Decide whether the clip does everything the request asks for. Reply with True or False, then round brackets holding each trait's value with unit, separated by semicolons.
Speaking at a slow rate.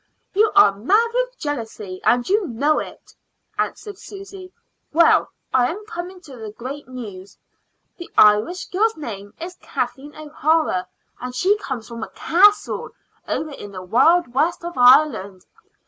False (145 wpm)